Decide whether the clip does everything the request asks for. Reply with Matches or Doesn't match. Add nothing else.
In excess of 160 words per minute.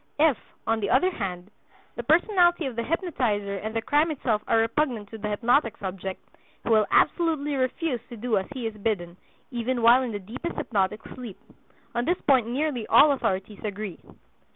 Matches